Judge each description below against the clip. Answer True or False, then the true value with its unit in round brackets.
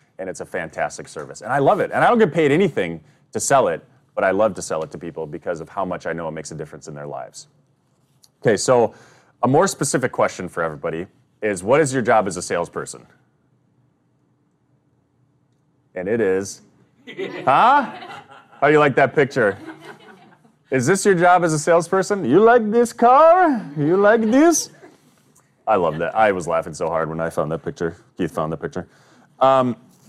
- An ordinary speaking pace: True (195 wpm)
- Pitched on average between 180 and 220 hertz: False (140 Hz)